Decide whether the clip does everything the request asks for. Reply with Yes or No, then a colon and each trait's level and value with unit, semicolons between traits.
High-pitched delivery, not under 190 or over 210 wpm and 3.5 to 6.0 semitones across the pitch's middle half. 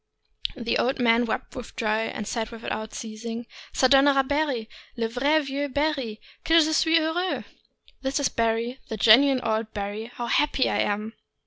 No: high, 240 Hz; average, 175 wpm; average, 4.1 semitones